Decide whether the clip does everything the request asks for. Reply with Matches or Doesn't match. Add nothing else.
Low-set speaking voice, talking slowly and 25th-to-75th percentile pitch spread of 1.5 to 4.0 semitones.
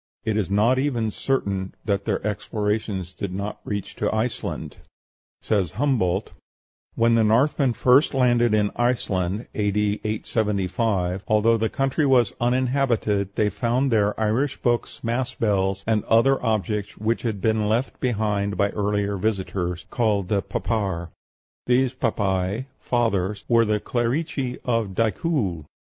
Matches